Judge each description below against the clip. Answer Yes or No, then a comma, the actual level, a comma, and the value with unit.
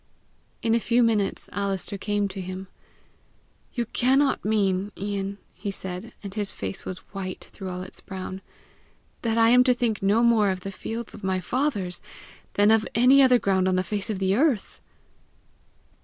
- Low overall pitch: No, high, 205 Hz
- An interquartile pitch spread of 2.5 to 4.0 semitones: Yes, average, 3.4 semitones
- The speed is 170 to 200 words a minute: Yes, average, 175 wpm